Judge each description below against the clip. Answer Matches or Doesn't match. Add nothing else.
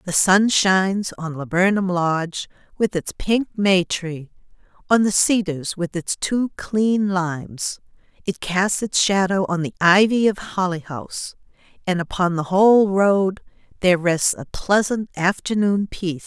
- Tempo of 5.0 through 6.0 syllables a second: Doesn't match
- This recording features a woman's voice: Matches